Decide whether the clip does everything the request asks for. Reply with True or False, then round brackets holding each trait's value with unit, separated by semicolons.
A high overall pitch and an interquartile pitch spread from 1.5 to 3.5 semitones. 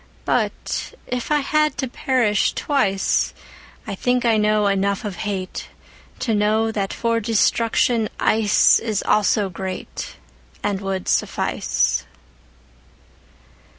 True (210 Hz; 2.9 semitones)